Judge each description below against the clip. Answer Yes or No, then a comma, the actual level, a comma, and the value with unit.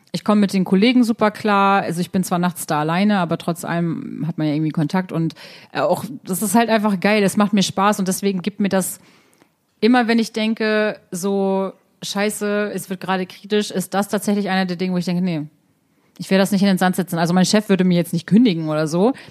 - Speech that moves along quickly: Yes, fast, 235 wpm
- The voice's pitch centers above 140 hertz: Yes, high, 190 Hz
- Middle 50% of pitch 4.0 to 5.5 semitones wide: No, narrow, 2.6 semitones